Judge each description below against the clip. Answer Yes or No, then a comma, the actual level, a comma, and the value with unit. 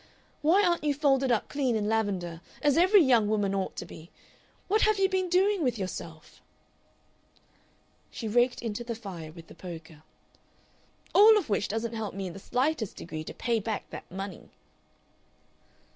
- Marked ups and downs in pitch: Yes, wide, 7.5 semitones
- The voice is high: Yes, high, 225 Hz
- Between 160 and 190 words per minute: Yes, average, 170 wpm